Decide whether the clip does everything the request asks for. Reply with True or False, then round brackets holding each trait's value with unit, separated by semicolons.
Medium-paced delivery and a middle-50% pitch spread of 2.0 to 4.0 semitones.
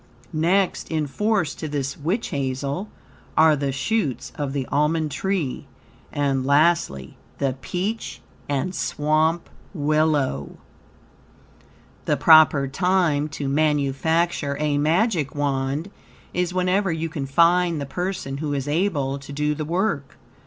False (125 wpm; 3.6 semitones)